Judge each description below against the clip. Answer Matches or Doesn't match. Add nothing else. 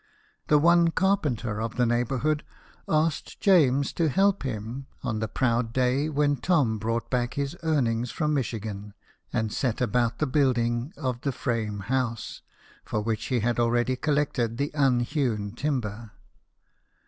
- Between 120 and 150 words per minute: Matches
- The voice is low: Matches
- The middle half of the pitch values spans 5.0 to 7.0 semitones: Doesn't match